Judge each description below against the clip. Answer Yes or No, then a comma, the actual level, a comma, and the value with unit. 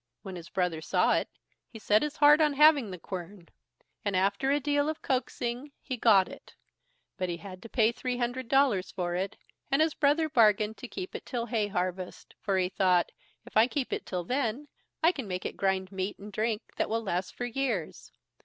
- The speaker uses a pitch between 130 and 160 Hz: No, high, 220 Hz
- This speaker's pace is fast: Yes, fast, 210 wpm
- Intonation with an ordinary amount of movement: No, wide, 6.3 semitones